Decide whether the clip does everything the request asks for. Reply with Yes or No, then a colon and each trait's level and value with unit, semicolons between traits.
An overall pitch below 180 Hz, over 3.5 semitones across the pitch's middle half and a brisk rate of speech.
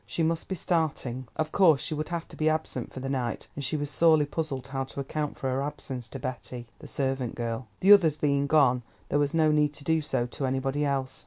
No: medium, 140 Hz; average, 3.0 semitones; fast, 240 wpm